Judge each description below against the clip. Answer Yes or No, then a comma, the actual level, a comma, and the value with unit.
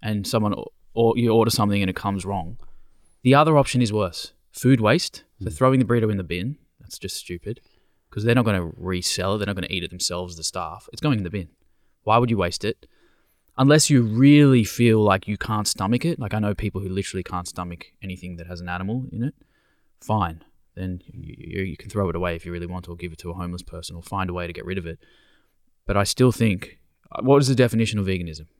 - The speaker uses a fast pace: Yes, fast, 245 wpm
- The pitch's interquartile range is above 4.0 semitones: Yes, average, 4.4 semitones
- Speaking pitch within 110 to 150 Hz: No, low, 100 Hz